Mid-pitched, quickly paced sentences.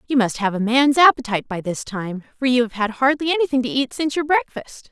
No: very high, 250 Hz; fast, 245 wpm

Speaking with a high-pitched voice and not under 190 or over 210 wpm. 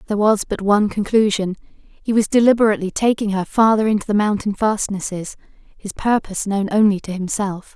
No: high, 205 Hz; average, 160 wpm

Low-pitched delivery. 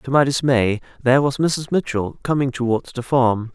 Yes: low, 130 Hz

